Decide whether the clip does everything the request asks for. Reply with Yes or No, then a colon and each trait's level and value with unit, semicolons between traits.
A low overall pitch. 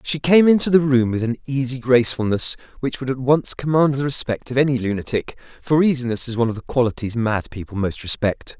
Yes: low, 130 Hz